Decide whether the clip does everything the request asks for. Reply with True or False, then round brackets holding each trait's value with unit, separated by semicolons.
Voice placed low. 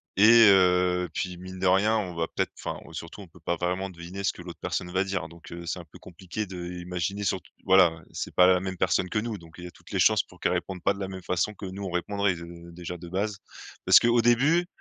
True (90 Hz)